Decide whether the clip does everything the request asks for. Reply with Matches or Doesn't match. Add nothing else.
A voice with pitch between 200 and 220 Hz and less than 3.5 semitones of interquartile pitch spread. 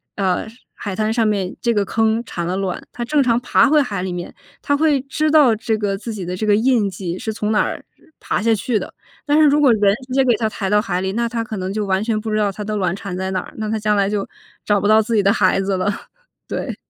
Matches